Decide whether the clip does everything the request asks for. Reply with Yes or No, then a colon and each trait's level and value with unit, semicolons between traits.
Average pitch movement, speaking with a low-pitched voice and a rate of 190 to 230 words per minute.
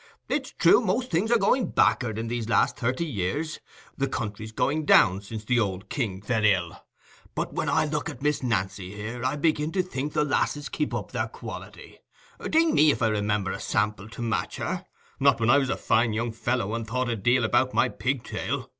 No: wide, 5.7 semitones; low, 120 Hz; average, 200 wpm